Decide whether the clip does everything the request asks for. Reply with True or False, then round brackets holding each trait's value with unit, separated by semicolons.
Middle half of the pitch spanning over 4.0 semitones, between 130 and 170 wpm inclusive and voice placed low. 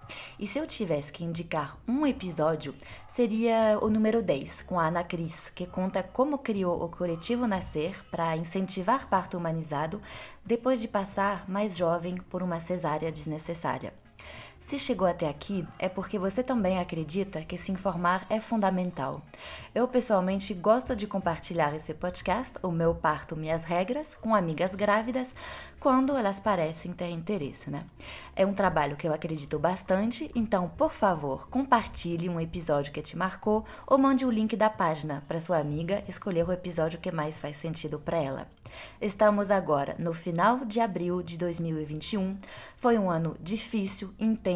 False (4.4 semitones; 160 wpm; 185 Hz)